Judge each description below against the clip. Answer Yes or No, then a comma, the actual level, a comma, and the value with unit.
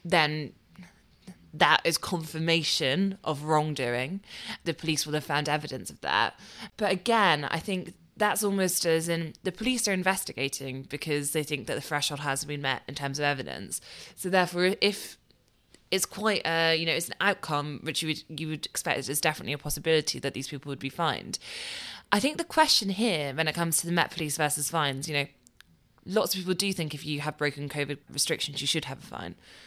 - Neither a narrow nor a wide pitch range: Yes, average, 3.9 semitones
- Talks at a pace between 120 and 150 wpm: No, average, 200 wpm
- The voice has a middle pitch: Yes, medium, 155 Hz